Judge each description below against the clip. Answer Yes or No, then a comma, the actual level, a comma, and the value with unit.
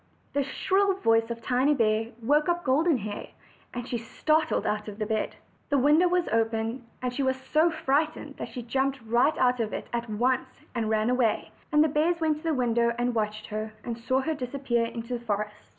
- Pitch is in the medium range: No, very high, 250 Hz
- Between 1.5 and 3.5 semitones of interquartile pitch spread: No, average, 4.6 semitones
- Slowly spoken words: No, fast, 205 wpm